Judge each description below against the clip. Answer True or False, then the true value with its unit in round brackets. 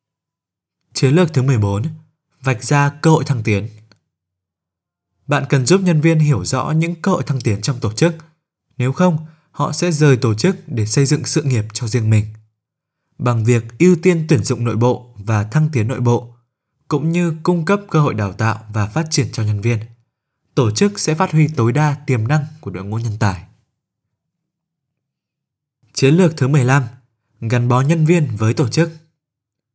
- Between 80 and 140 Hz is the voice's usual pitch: True (135 Hz)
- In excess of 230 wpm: False (185 wpm)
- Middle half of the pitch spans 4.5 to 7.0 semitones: True (5.5 semitones)